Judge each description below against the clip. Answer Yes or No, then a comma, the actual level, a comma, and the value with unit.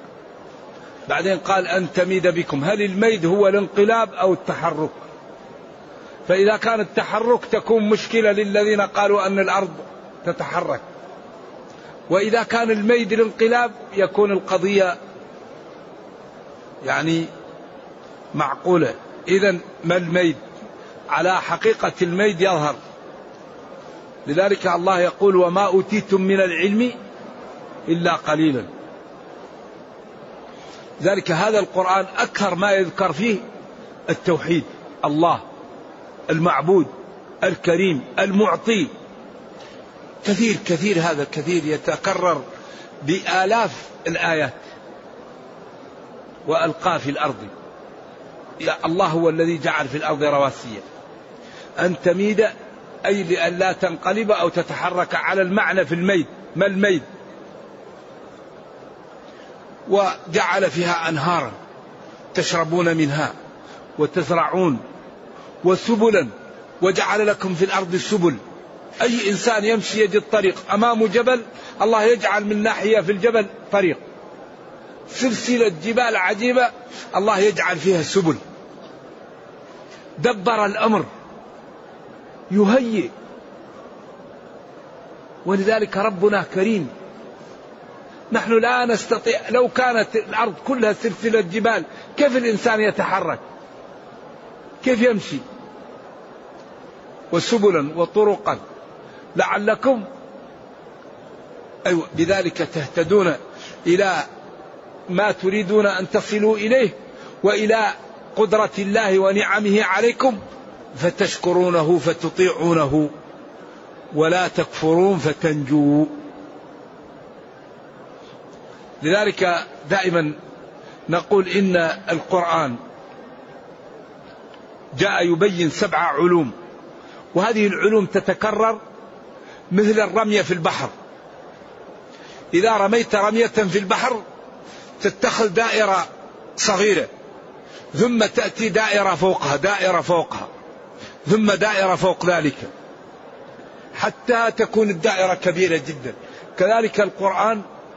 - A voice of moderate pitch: No, high, 195 Hz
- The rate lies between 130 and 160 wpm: No, average, 85 wpm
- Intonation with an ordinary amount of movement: Yes, average, 3.8 semitones